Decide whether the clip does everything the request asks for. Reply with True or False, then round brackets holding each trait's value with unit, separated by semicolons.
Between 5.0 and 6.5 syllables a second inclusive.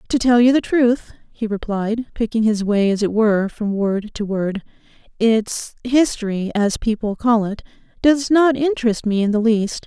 False (4.6 syllables/s)